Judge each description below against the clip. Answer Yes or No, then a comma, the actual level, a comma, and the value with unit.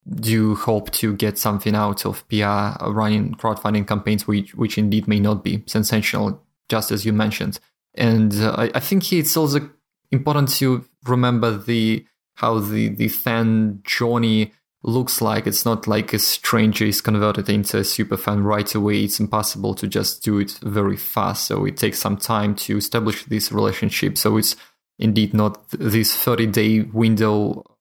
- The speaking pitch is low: Yes, low, 110 Hz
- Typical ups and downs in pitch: No, narrow, 1.5 semitones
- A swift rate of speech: No, average, 170 wpm